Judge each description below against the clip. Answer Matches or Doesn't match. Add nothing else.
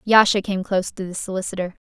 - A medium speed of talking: Matches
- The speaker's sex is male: Doesn't match